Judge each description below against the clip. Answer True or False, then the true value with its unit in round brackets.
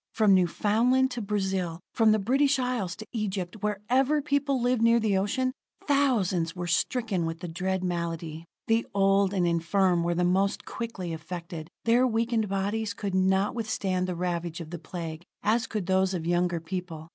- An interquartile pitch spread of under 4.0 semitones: False (4.4 semitones)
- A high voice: True (195 Hz)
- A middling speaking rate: True (170 wpm)